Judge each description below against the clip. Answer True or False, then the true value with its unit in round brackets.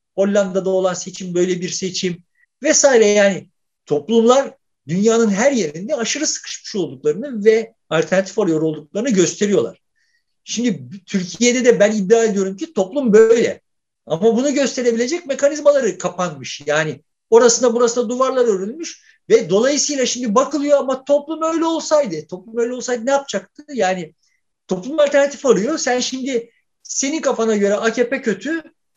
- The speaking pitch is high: True (230 Hz)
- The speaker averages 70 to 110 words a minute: False (130 wpm)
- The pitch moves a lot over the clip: True (6.3 semitones)